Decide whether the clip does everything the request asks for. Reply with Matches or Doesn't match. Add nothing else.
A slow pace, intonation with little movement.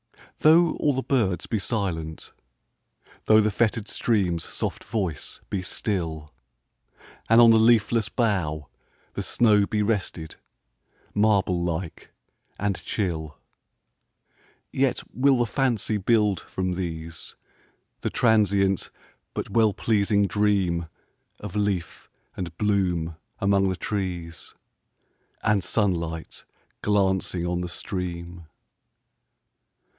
Doesn't match